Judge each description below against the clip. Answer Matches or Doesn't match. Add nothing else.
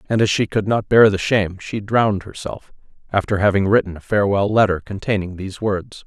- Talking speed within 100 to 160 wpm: Doesn't match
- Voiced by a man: Matches